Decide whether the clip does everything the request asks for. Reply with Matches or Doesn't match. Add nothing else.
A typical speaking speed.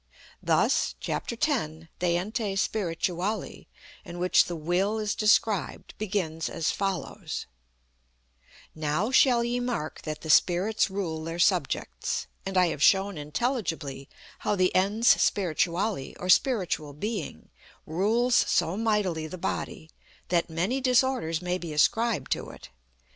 Doesn't match